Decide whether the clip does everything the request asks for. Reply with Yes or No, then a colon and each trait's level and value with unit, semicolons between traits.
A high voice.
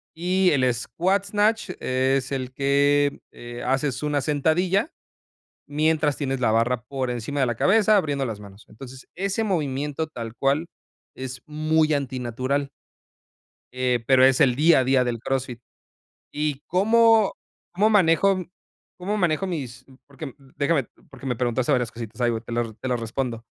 No: low, 135 Hz